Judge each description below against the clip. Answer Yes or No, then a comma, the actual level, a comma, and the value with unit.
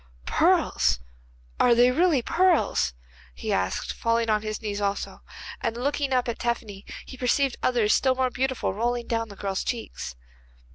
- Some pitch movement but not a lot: Yes, average, 3.6 semitones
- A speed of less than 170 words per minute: Yes, average, 155 wpm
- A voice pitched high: Yes, high, 235 Hz